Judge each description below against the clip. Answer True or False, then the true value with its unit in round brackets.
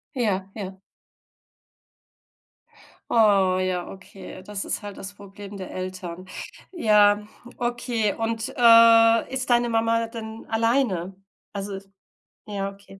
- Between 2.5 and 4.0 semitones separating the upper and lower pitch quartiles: True (2.8 semitones)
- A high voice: True (205 Hz)